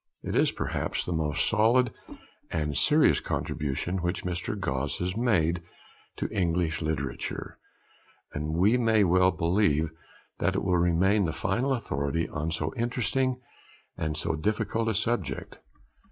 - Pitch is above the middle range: No, very low, 90 Hz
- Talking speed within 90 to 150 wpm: Yes, average, 140 wpm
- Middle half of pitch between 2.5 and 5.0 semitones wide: No, wide, 5.4 semitones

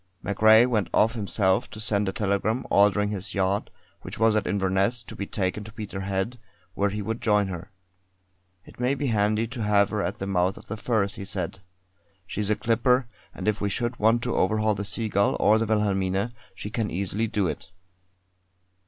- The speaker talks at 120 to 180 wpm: No, average, 190 wpm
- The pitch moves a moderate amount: No, narrow, 2.1 semitones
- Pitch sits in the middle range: No, low, 105 Hz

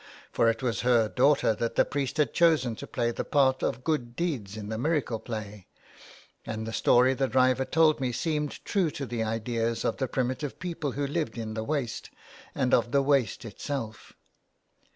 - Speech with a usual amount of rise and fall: Yes, average, 4.2 semitones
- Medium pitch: No, low, 125 Hz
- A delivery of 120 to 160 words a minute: No, average, 190 wpm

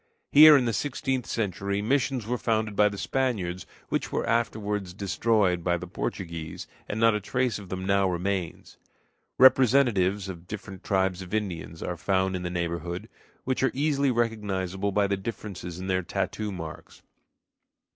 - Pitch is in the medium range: No, low, 100 Hz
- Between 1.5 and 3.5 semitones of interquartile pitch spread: No, average, 3.9 semitones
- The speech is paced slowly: No, average, 160 wpm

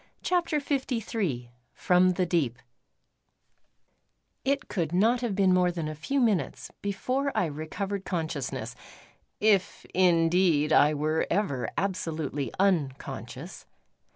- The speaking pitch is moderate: Yes, medium, 180 Hz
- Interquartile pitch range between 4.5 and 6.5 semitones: Yes, average, 5.1 semitones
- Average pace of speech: No, slow, 110 wpm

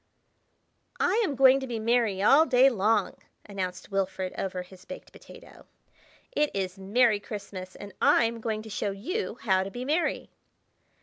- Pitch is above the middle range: Yes, high, 215 Hz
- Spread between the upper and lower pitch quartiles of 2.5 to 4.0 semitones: No, average, 4.8 semitones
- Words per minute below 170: Yes, average, 160 wpm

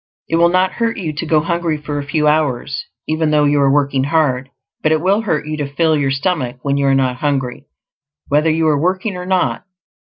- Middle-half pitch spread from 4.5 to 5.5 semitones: No, average, 2.8 semitones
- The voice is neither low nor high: Yes, medium, 150 Hz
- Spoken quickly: Yes, fast, 225 wpm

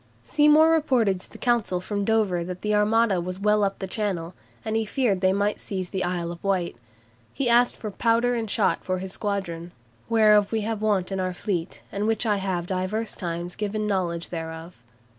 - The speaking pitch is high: Yes, high, 200 Hz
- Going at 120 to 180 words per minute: No, average, 195 wpm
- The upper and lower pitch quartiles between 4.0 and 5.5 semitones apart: No, average, 3.3 semitones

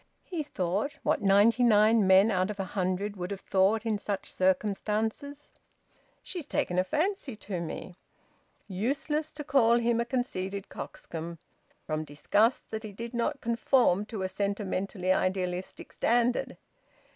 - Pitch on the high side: Yes, high, 210 Hz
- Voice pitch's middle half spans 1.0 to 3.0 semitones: No, average, 4.0 semitones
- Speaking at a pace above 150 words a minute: No, average, 145 wpm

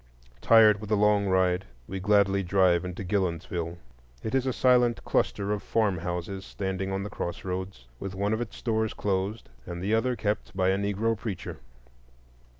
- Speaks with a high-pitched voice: No, low, 100 Hz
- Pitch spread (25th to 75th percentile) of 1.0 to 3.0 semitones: Yes, narrow, 2.5 semitones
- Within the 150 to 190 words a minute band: Yes, average, 165 wpm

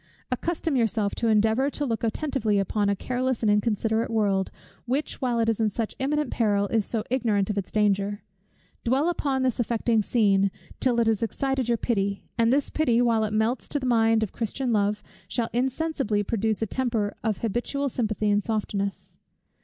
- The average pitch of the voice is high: Yes, high, 225 Hz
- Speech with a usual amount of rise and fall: Yes, average, 3.3 semitones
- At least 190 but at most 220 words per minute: No, average, 180 wpm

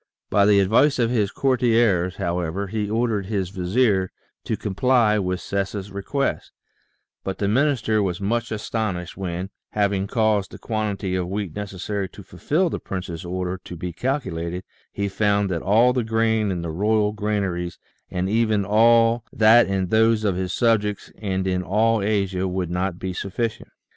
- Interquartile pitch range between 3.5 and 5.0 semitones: No, average, 3.1 semitones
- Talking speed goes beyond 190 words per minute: No, average, 165 wpm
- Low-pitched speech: Yes, low, 100 Hz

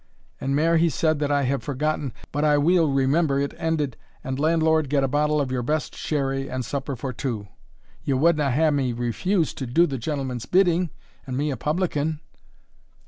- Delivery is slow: No, average, 195 wpm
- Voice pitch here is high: No, medium, 145 Hz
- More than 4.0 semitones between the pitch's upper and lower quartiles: No, average, 2.8 semitones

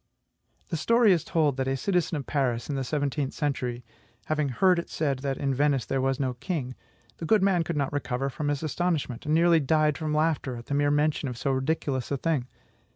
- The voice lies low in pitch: No, medium, 145 Hz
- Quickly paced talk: Yes, fast, 220 wpm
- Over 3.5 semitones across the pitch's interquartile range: No, average, 3.2 semitones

